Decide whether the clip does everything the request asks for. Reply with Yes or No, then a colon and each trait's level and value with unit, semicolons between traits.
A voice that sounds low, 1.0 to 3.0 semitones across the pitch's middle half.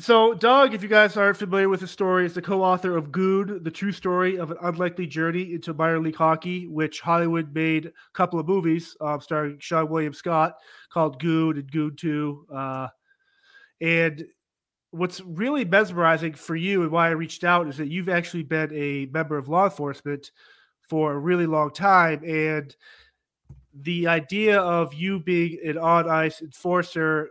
No: medium, 165 Hz; average, 2.7 semitones